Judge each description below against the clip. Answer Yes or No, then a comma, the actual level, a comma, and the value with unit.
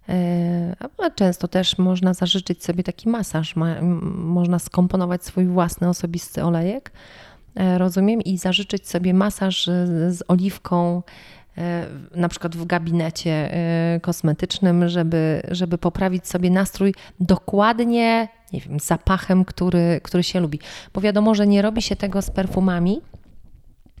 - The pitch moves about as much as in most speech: No, narrow, 1.8 semitones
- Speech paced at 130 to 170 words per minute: No, average, 120 wpm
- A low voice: No, medium, 180 Hz